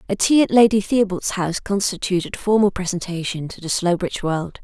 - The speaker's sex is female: Yes, female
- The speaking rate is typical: Yes, average, 170 wpm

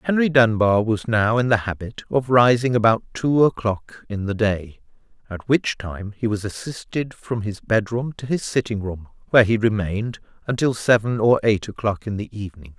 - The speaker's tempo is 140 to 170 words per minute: No, average, 185 wpm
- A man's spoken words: Yes, male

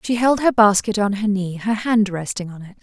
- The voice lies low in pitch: No, high, 210 Hz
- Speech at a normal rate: No, fast, 255 wpm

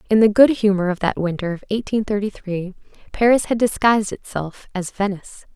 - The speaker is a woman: Yes, female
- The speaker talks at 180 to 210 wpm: Yes, average, 185 wpm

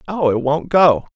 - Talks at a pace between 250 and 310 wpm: No, fast, 205 wpm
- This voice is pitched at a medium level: Yes, medium, 155 Hz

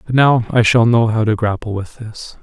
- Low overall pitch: Yes, low, 115 Hz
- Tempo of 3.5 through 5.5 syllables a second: Yes, 5.1 syllables/s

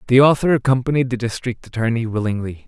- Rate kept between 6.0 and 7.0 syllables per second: Yes, 6.5 syllables/s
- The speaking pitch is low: Yes, low, 120 Hz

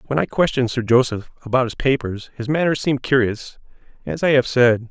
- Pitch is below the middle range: Yes, low, 125 Hz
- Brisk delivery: No, average, 195 wpm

